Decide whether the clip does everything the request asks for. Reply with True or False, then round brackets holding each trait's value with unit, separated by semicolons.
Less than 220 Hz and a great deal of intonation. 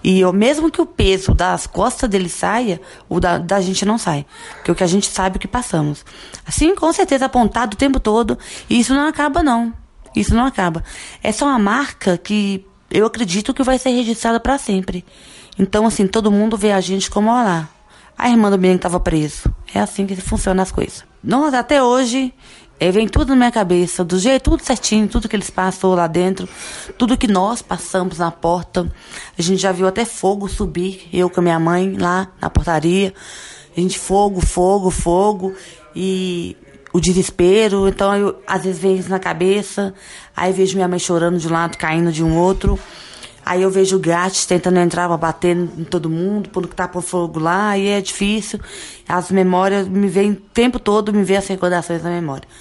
False (190 Hz; 3.3 semitones)